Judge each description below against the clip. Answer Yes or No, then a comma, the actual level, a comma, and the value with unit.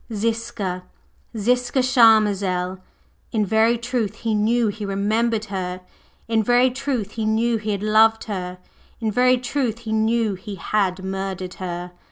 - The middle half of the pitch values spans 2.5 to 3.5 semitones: Yes, average, 3.1 semitones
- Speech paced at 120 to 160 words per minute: Yes, average, 145 wpm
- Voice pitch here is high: Yes, high, 220 Hz